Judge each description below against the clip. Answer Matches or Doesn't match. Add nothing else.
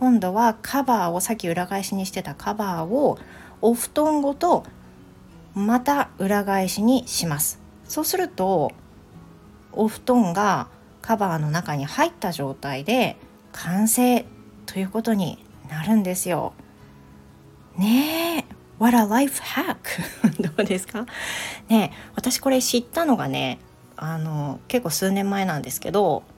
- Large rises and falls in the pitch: Matches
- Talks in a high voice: Matches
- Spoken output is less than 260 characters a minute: Matches